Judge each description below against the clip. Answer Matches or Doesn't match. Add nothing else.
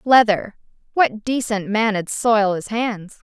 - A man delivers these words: Doesn't match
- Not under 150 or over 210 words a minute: Doesn't match